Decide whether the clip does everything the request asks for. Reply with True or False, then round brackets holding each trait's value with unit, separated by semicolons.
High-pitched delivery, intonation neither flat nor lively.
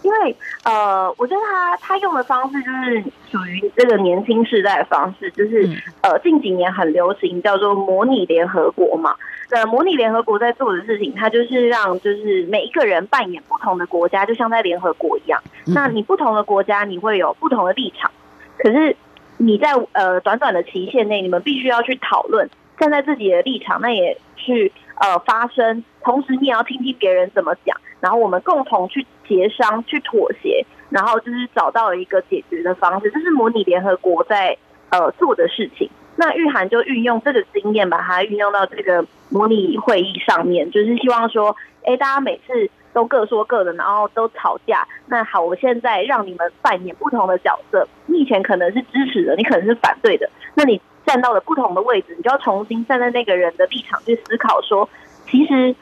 False (235 Hz; 6.0 semitones)